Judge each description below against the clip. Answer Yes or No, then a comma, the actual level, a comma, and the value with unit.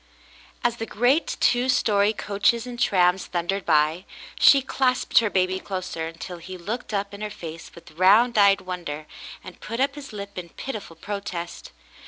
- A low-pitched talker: No, high, 200 Hz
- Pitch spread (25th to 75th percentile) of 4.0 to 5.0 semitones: Yes, average, 4.6 semitones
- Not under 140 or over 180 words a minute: Yes, average, 170 wpm